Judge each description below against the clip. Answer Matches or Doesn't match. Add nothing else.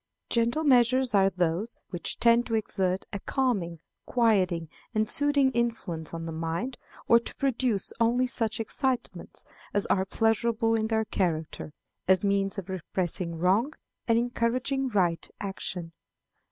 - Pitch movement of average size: Matches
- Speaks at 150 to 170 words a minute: Doesn't match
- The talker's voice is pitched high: Matches